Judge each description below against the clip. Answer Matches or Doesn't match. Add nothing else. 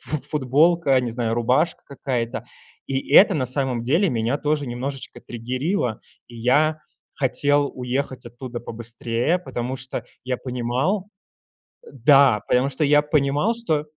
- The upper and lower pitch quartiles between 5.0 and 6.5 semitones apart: Doesn't match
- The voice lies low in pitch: Matches